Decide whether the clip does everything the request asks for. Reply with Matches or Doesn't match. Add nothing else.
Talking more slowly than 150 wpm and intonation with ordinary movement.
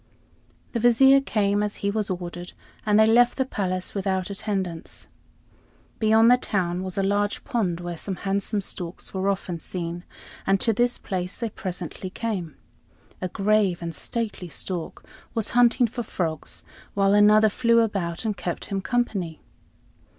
Doesn't match